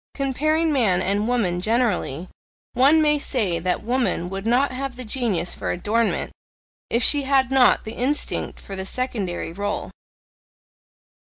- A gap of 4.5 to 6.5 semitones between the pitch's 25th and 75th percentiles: Yes, wide, 5.5 semitones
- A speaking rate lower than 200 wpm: Yes, average, 145 wpm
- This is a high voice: Yes, high, 235 Hz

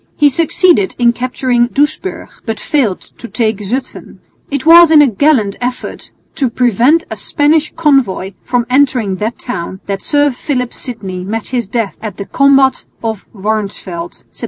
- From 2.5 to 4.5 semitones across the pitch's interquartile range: No, average, 5.3 semitones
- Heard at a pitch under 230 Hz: No, high, 245 Hz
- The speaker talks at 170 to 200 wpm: No, average, 160 wpm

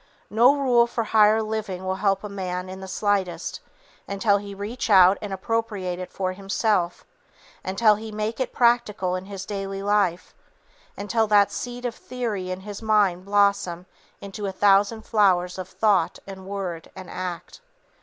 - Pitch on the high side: Yes, high, 200 Hz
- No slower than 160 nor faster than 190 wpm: Yes, average, 165 wpm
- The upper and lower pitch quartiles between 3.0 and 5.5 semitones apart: No, narrow, 2.5 semitones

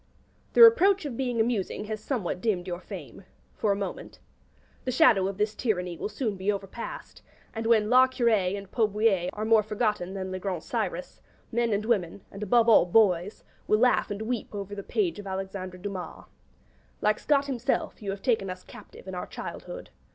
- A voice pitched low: No, high, 210 Hz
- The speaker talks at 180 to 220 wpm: Yes, average, 190 wpm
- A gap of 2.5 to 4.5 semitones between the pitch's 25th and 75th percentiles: Yes, average, 3.6 semitones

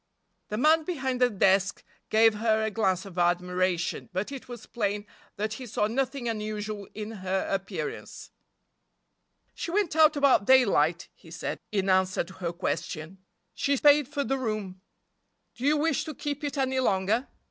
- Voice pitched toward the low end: No, high, 215 Hz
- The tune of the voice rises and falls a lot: Yes, wide, 5.9 semitones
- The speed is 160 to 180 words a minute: Yes, average, 165 wpm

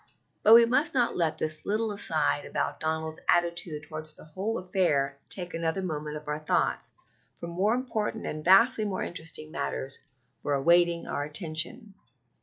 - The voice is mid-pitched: Yes, medium, 170 Hz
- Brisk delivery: No, average, 160 wpm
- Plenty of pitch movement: No, average, 4.8 semitones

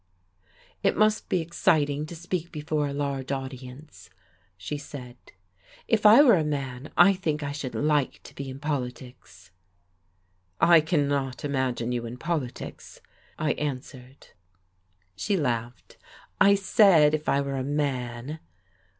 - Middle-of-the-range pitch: Yes, medium, 145 Hz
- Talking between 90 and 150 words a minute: Yes, slow, 135 wpm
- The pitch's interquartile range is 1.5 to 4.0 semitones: Yes, average, 3.4 semitones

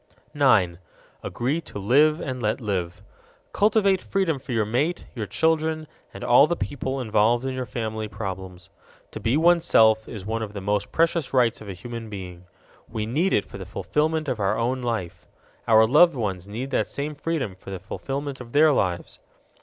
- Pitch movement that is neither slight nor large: No, wide, 6.2 semitones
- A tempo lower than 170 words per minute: No, average, 185 wpm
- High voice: No, low, 120 Hz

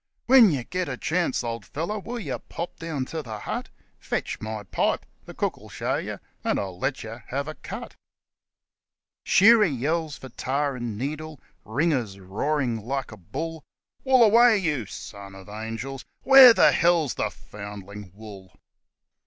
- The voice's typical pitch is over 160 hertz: No, low, 135 Hz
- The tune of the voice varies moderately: No, wide, 7.2 semitones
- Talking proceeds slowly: No, average, 170 wpm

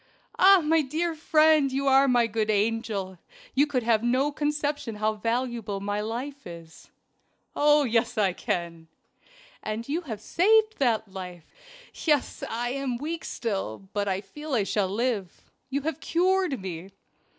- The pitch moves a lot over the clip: Yes, wide, 6.2 semitones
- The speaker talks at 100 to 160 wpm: Yes, average, 150 wpm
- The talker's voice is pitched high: Yes, high, 240 Hz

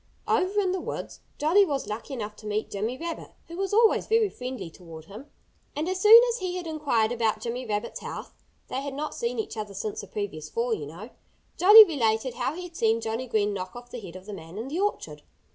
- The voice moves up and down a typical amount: No, wide, 8.0 semitones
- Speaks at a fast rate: Yes, fast, 230 wpm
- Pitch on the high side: Yes, high, 245 Hz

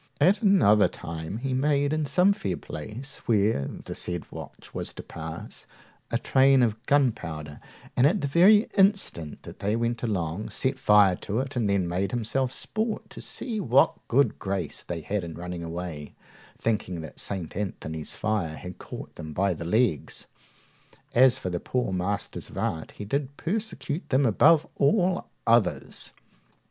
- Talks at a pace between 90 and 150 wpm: No, average, 165 wpm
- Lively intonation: Yes, wide, 7.7 semitones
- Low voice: Yes, low, 110 Hz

